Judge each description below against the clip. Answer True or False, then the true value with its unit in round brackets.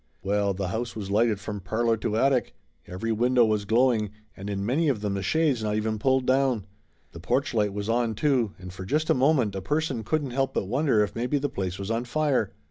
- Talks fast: True (225 wpm)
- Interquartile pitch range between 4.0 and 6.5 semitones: True (4.4 semitones)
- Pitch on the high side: False (115 Hz)